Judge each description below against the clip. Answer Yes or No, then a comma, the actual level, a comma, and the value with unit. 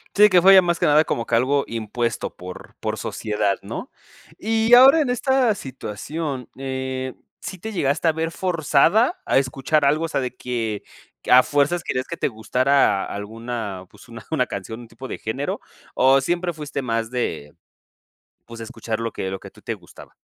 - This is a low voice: Yes, low, 130 Hz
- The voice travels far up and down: Yes, wide, 6.3 semitones